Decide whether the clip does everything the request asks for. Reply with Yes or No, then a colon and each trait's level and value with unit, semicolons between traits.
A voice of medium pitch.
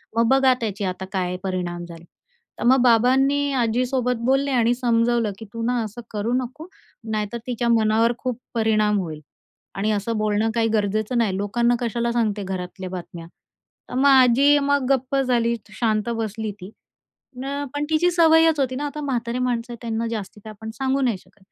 No: high, 235 Hz